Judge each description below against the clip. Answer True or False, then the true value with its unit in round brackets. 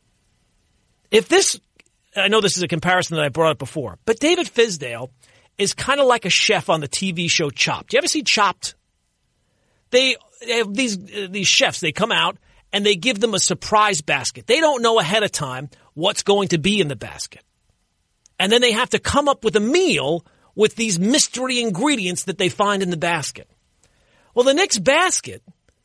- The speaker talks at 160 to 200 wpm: True (195 wpm)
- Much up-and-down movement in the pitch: True (6.6 semitones)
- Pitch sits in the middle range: False (200 Hz)